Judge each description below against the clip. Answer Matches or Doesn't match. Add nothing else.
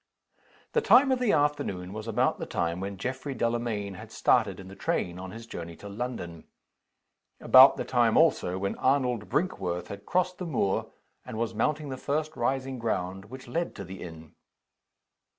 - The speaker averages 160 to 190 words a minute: Matches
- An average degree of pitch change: Doesn't match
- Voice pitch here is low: Matches